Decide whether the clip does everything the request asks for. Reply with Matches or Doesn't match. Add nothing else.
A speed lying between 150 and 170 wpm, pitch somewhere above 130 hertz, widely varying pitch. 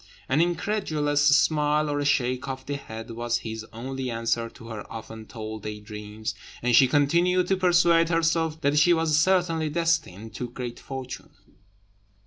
Matches